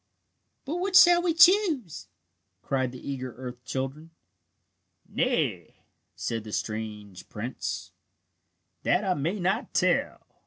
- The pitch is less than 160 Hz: Yes, medium, 140 Hz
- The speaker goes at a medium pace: No, slow, 115 wpm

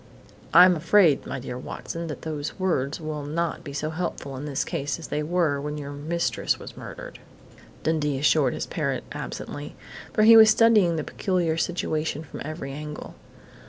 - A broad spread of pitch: No, average, 2.9 semitones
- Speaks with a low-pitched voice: No, medium, 155 Hz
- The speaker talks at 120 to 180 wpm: Yes, average, 170 wpm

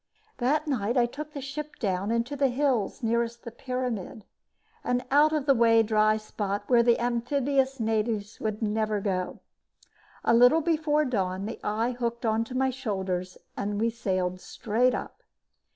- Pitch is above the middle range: Yes, high, 235 Hz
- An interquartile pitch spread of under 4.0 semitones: Yes, average, 3.6 semitones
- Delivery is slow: No, average, 160 wpm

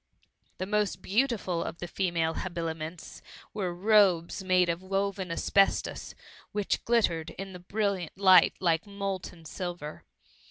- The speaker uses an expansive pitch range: No, average, 2.7 semitones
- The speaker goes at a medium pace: No, slow, 125 wpm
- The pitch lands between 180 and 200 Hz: Yes, medium, 185 Hz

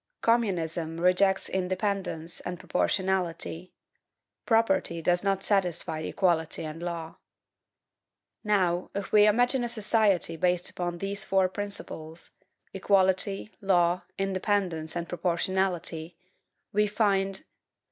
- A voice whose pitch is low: No, medium, 185 Hz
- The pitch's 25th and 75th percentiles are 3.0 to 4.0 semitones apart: No, narrow, 2.6 semitones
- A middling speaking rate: No, slow, 105 wpm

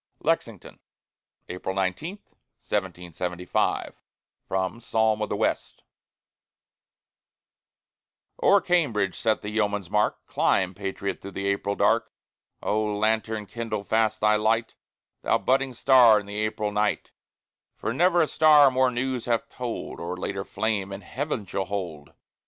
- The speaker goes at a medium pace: No, slow, 130 wpm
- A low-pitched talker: Yes, low, 105 Hz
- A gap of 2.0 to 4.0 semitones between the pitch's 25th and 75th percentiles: Yes, average, 3.3 semitones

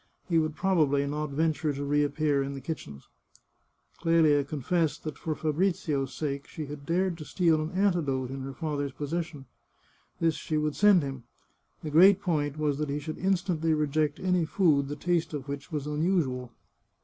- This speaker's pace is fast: No, average, 175 wpm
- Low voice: No, medium, 150 Hz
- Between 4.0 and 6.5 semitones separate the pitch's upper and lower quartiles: No, average, 2.7 semitones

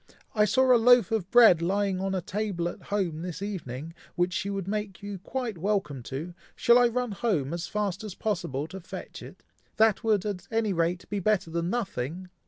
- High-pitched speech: Yes, high, 195 Hz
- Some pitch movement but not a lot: Yes, average, 3.9 semitones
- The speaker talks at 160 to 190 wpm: No, average, 200 wpm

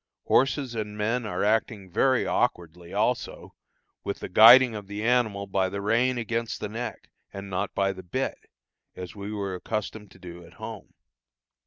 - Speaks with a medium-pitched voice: No, low, 105 Hz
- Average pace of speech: Yes, average, 170 wpm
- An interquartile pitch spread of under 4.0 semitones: Yes, average, 3.2 semitones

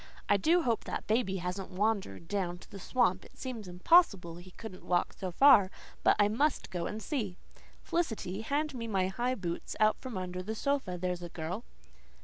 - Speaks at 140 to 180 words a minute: No, average, 190 wpm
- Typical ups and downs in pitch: Yes, average, 4.8 semitones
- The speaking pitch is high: Yes, high, 200 Hz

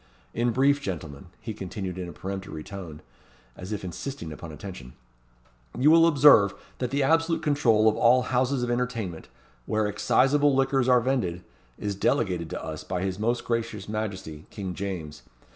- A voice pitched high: No, low, 105 Hz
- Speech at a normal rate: Yes, average, 160 wpm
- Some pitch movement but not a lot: No, wide, 5.8 semitones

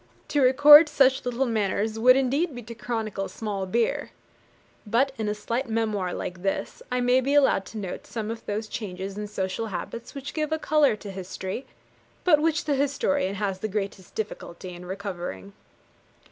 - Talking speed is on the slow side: No, average, 175 wpm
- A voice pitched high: Yes, high, 225 Hz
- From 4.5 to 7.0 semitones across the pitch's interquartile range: Yes, average, 5.2 semitones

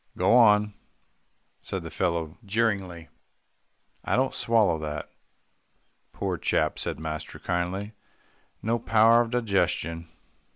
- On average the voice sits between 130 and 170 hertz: No, very low, 95 Hz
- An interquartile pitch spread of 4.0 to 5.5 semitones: Yes, average, 5.2 semitones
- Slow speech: Yes, slow, 110 wpm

